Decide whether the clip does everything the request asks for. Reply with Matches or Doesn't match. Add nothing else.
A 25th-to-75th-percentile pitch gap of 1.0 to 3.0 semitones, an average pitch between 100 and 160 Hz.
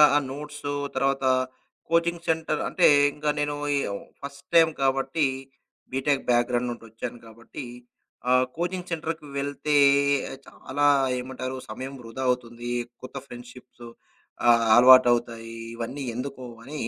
Doesn't match